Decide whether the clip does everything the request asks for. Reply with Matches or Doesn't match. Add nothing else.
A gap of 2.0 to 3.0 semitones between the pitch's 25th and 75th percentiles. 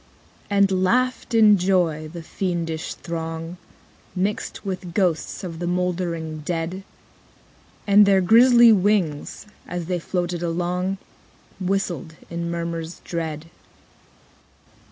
Matches